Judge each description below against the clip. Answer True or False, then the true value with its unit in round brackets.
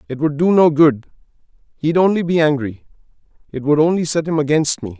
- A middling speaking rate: True (190 wpm)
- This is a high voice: False (155 Hz)